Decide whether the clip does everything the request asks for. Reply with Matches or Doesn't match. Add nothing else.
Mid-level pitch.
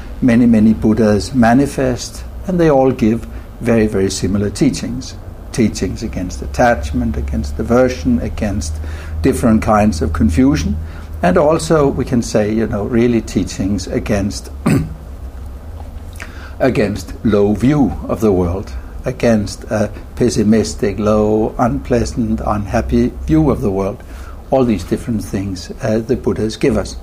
Doesn't match